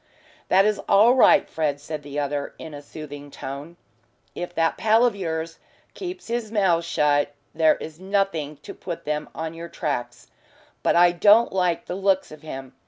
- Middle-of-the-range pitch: Yes, medium, 165 Hz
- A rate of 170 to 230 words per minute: Yes, average, 175 wpm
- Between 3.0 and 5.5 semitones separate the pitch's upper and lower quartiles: Yes, average, 4.7 semitones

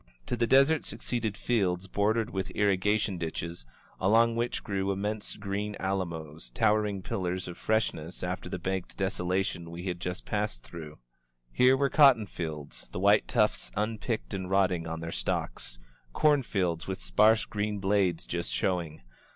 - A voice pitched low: Yes, very low, 95 Hz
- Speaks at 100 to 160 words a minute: Yes, average, 155 wpm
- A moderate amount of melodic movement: Yes, average, 3.7 semitones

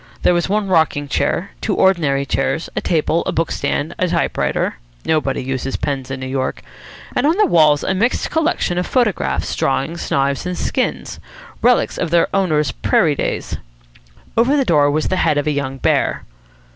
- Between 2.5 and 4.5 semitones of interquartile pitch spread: No, average, 5.2 semitones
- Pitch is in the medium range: Yes, medium, 160 Hz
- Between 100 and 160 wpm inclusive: No, average, 180 wpm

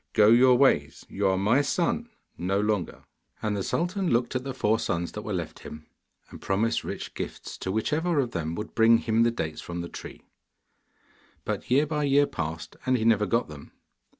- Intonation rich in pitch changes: Yes, wide, 5.7 semitones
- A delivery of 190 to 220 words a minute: Yes, average, 200 wpm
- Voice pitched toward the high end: No, low, 110 Hz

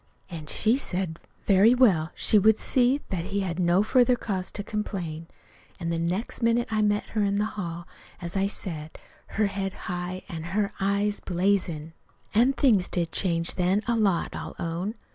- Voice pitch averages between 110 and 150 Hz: No, high, 195 Hz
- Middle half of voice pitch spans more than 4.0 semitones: No, average, 3.7 semitones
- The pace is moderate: Yes, average, 180 wpm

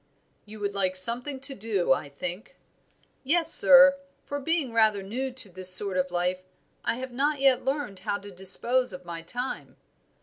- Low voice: No, high, 220 Hz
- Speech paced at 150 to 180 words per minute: Yes, average, 175 wpm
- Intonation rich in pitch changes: Yes, wide, 6.3 semitones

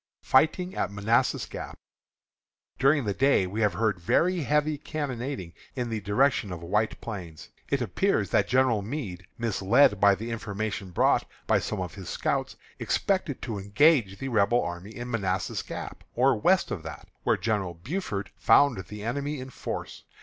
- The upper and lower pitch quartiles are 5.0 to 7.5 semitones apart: Yes, wide, 5.6 semitones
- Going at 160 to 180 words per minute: Yes, average, 165 wpm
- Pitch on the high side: No, low, 110 Hz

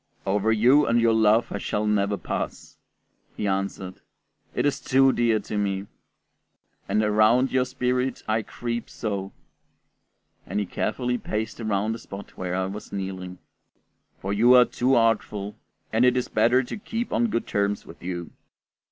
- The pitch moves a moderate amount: Yes, average, 3.6 semitones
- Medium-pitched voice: No, low, 110 Hz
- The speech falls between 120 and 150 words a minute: No, average, 160 wpm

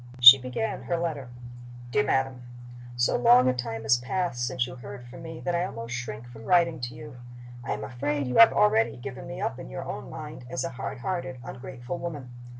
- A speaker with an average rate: No, fast, 210 wpm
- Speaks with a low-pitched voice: Yes, low, 130 Hz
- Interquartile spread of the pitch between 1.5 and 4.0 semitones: Yes, average, 3.4 semitones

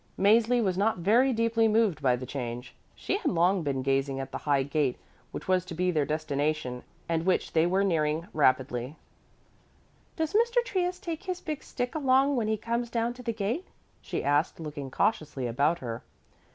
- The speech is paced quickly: No, average, 185 wpm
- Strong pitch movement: Yes, wide, 8.6 semitones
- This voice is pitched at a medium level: Yes, medium, 180 Hz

